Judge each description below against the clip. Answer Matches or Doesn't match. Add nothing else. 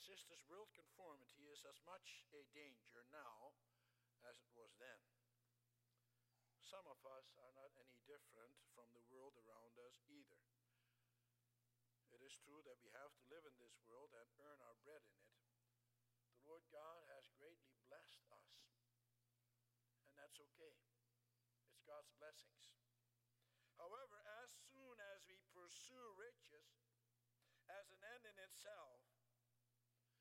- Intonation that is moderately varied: Matches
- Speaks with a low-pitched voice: Matches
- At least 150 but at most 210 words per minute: Doesn't match